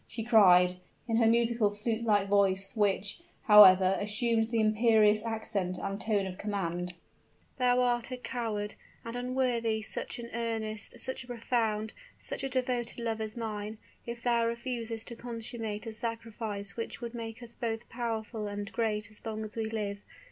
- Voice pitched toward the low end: No, high, 225 Hz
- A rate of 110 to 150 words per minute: No, average, 165 wpm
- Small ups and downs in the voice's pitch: Yes, narrow, 2.1 semitones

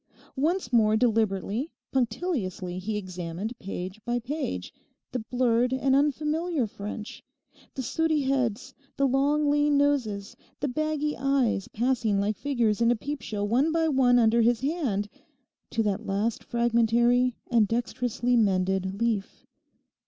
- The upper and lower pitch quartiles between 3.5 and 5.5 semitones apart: Yes, average, 4.6 semitones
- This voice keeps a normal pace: No, slow, 125 wpm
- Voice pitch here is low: No, high, 240 Hz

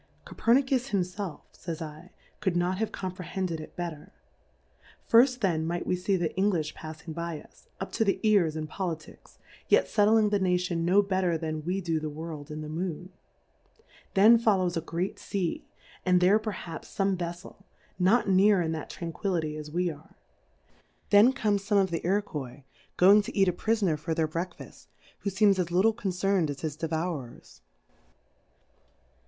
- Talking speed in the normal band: Yes, average, 170 wpm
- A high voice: No, medium, 180 Hz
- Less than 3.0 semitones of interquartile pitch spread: No, average, 3.6 semitones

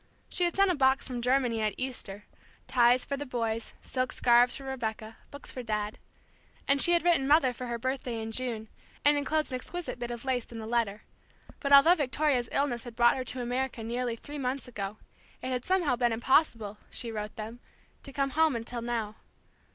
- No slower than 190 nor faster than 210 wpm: Yes, average, 200 wpm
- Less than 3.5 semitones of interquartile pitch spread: Yes, average, 3.1 semitones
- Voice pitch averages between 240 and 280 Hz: Yes, very high, 250 Hz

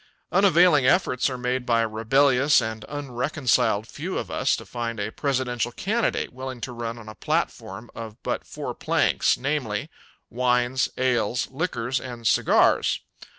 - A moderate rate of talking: Yes, average, 150 wpm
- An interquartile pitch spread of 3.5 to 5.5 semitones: No, average, 2.8 semitones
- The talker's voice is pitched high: No, low, 125 Hz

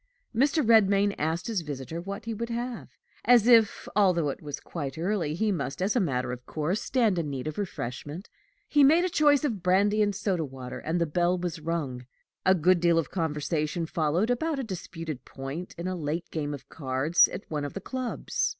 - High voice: No, medium, 175 Hz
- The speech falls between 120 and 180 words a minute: No, average, 200 wpm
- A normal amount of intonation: No, wide, 5.8 semitones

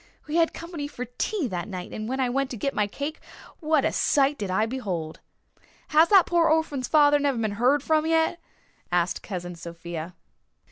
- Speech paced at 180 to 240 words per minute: Yes, average, 190 wpm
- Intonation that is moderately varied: No, wide, 7.5 semitones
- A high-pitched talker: Yes, very high, 265 Hz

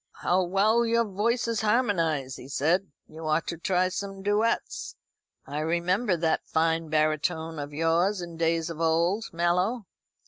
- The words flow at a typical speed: Yes, average, 145 wpm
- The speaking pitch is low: No, medium, 175 Hz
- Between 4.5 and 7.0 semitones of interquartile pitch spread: No, average, 3.9 semitones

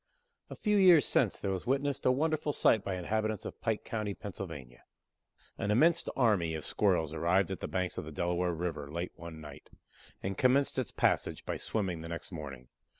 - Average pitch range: No, wide, 6.6 semitones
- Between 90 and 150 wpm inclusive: No, average, 190 wpm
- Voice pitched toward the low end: Yes, very low, 95 Hz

